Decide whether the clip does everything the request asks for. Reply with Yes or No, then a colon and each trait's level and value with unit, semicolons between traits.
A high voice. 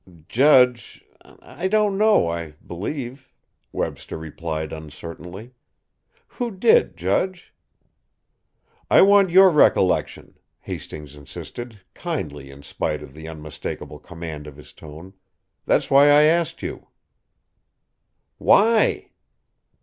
No: low, 105 Hz